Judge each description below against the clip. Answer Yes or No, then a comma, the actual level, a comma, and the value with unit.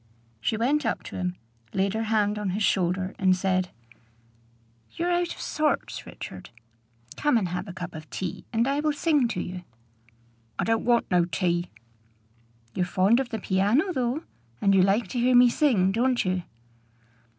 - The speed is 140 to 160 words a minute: No, average, 175 wpm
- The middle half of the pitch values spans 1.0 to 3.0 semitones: No, average, 5.2 semitones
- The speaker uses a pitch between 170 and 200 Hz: No, high, 210 Hz